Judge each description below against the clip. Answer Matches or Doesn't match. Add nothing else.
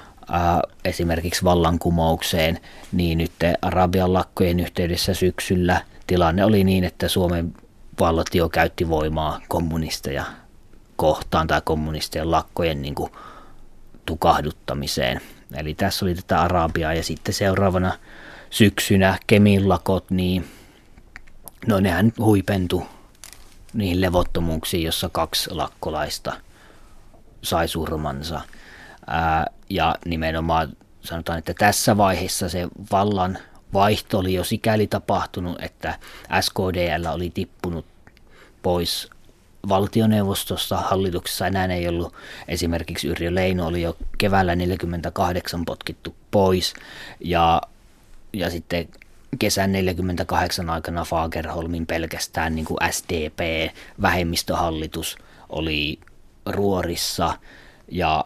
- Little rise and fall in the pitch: Matches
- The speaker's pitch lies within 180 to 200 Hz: Doesn't match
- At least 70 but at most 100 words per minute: Matches